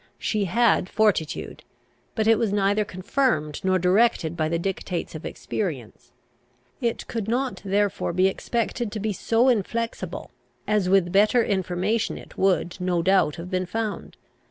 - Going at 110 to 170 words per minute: Yes, average, 150 wpm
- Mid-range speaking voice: No, high, 195 Hz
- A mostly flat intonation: No, average, 3.6 semitones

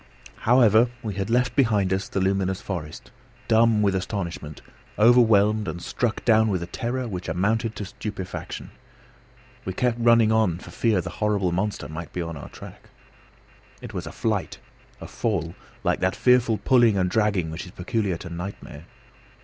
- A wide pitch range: No, average, 3.8 semitones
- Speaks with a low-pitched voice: Yes, low, 100 Hz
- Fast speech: No, average, 165 wpm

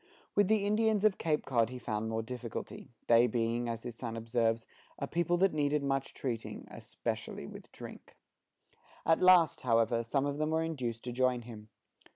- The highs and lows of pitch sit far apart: Yes, wide, 5.7 semitones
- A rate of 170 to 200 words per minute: Yes, average, 180 wpm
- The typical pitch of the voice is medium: No, low, 125 Hz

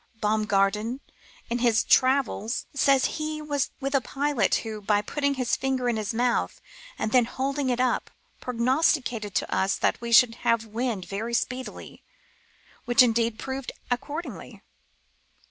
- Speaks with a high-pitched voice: Yes, high, 245 Hz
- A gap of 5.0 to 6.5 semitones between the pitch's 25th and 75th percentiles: No, average, 3.3 semitones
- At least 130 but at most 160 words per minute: Yes, average, 145 wpm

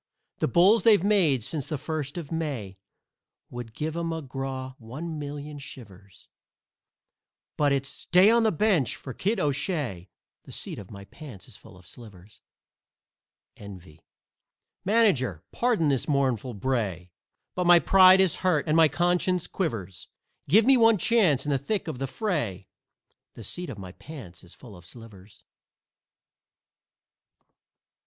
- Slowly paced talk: No, average, 145 wpm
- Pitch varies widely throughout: Yes, wide, 8.3 semitones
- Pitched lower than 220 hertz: Yes, medium, 140 Hz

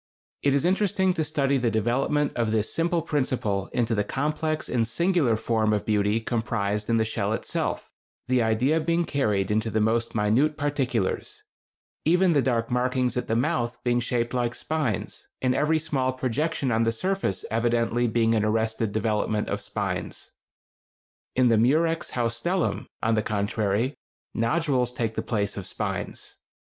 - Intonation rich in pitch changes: No, average, 4.7 semitones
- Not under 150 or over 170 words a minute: Yes, average, 155 wpm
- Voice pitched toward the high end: No, low, 120 Hz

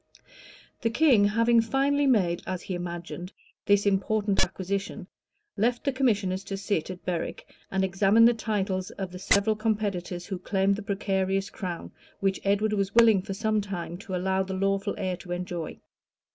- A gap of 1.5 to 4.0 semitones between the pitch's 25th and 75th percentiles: Yes, narrow, 2.5 semitones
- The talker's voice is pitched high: Yes, high, 195 Hz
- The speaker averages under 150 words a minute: No, average, 165 wpm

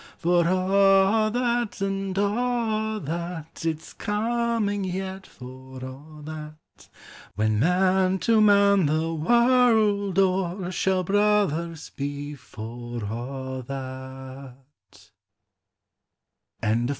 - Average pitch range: No, wide, 6.7 semitones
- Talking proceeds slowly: Yes, slow, 95 wpm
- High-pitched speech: No, medium, 180 Hz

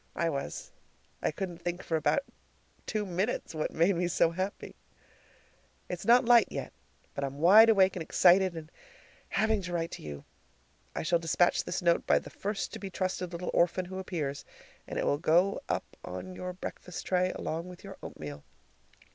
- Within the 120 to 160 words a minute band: No, average, 180 wpm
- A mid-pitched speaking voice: Yes, medium, 180 Hz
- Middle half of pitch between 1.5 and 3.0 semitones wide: Yes, narrow, 2.5 semitones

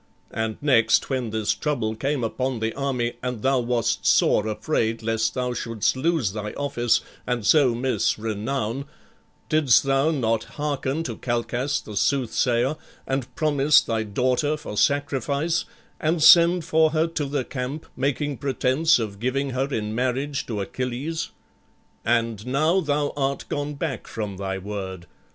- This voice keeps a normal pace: Yes, average, 150 wpm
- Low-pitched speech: Yes, low, 130 Hz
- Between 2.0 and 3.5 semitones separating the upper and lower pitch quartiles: No, average, 4.2 semitones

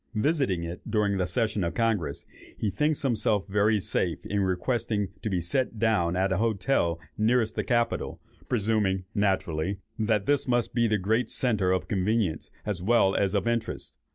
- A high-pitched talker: No, low, 105 Hz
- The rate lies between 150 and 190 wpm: Yes, average, 170 wpm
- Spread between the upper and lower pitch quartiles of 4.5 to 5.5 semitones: No, average, 3.6 semitones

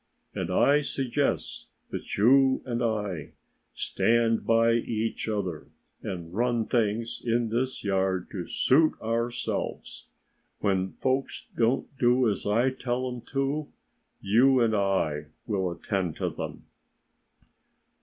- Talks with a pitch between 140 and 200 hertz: No, low, 115 Hz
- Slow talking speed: Yes, slow, 120 wpm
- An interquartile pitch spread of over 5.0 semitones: No, average, 4.3 semitones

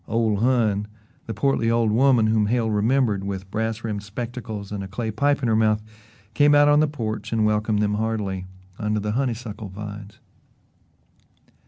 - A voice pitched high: No, low, 110 Hz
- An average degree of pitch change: No, narrow, 2.2 semitones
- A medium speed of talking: Yes, average, 170 wpm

